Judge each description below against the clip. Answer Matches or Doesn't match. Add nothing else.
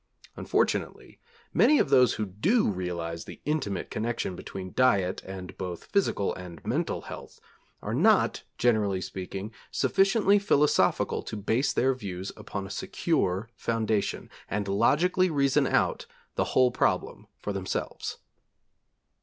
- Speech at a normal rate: Doesn't match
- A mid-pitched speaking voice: Doesn't match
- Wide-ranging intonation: Matches